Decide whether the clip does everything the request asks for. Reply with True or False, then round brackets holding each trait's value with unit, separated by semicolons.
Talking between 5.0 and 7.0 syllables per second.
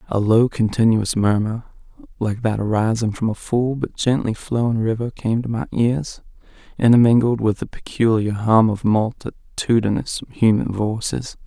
False (4.6 syllables/s)